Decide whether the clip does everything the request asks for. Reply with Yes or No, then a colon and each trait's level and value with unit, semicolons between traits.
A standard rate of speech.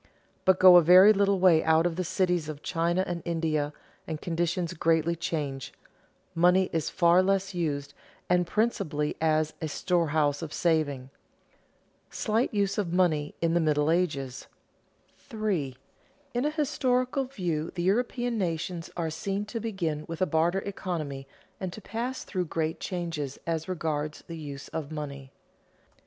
Yes: average, 155 wpm